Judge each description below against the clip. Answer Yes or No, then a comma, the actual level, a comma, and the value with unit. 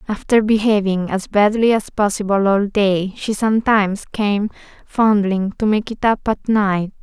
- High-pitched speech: Yes, high, 205 Hz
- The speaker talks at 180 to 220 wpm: No, average, 155 wpm